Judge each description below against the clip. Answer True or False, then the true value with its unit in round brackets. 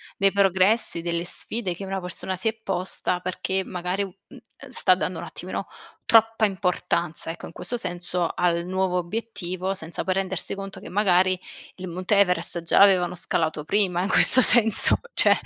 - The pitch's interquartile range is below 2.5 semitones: True (2.0 semitones)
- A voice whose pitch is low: False (185 Hz)